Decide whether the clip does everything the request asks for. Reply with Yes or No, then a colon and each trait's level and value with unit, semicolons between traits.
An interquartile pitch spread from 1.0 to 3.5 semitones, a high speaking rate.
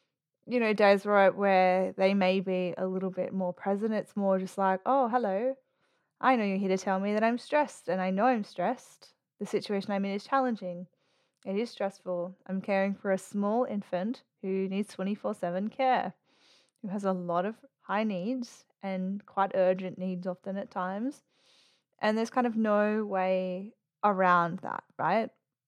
No: average, 2.7 semitones; average, 180 wpm